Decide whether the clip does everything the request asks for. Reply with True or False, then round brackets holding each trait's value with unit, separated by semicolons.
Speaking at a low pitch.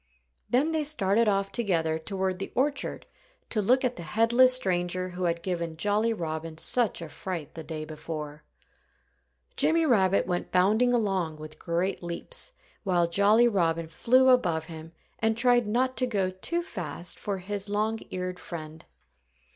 False (190 Hz)